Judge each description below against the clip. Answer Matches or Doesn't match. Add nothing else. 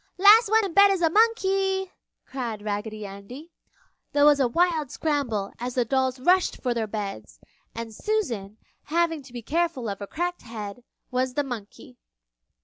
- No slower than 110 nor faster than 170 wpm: Matches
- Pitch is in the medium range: Doesn't match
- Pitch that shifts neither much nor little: Doesn't match